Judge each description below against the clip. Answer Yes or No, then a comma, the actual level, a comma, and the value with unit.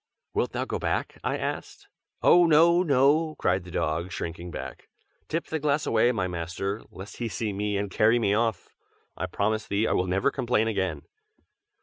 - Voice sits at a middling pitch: No, low, 105 Hz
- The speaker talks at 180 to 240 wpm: Yes, average, 185 wpm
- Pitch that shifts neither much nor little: No, wide, 6.7 semitones